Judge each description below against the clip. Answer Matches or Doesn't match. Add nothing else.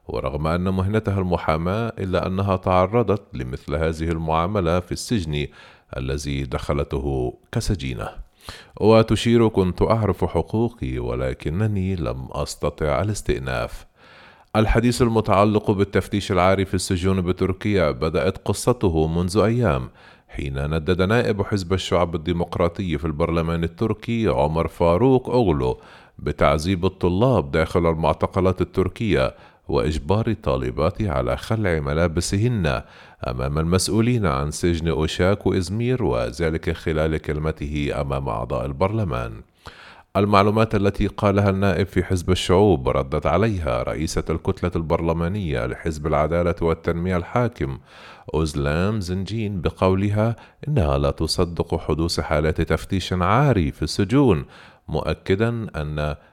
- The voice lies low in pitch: Matches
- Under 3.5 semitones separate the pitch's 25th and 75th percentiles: Doesn't match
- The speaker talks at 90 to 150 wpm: Matches